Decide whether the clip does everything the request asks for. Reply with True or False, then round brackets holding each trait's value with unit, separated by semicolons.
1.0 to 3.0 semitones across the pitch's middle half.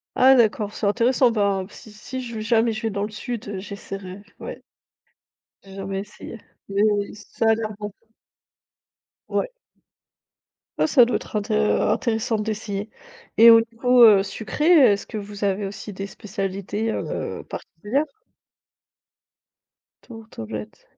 True (2.4 semitones)